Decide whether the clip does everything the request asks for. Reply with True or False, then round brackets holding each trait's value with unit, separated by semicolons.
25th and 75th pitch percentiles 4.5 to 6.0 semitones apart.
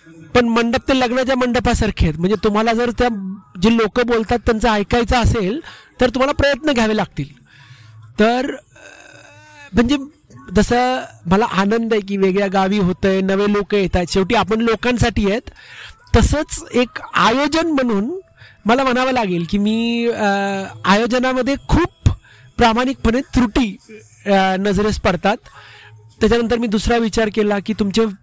False (3.8 semitones)